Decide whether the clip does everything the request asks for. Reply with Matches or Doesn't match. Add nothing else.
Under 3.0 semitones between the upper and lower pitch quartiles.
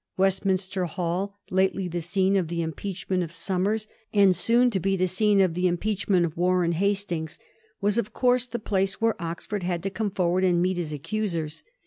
Matches